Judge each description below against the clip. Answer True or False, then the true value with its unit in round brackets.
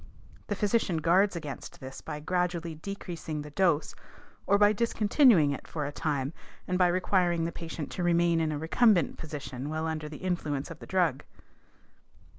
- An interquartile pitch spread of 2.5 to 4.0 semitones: True (3.4 semitones)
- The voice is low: False (170 Hz)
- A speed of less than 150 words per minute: False (170 wpm)